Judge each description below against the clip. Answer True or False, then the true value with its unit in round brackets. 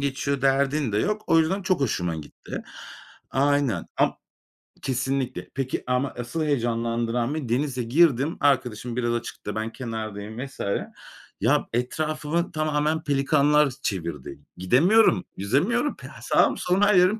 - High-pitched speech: False (135 Hz)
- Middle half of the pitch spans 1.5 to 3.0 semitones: False (4.6 semitones)